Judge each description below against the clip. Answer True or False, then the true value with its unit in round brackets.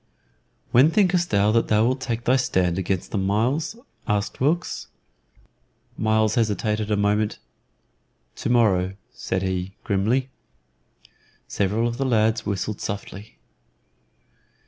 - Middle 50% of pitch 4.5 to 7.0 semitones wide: False (3.3 semitones)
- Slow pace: True (120 wpm)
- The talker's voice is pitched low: True (110 Hz)